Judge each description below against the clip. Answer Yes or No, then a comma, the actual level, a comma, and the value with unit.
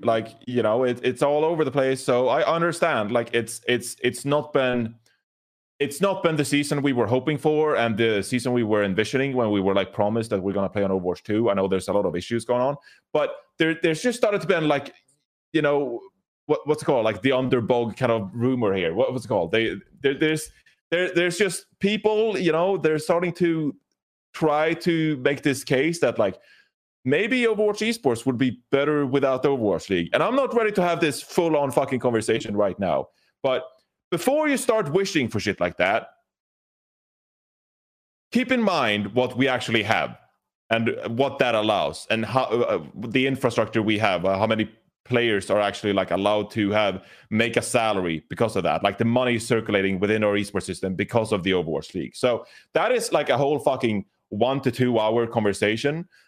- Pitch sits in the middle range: No, low, 130 Hz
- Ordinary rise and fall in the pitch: No, wide, 6.0 semitones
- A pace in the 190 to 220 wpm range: Yes, fast, 205 wpm